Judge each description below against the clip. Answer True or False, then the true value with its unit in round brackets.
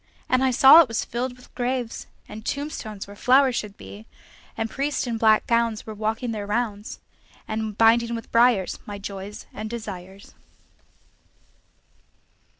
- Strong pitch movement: False (2.7 semitones)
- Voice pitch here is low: False (225 Hz)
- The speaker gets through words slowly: False (150 wpm)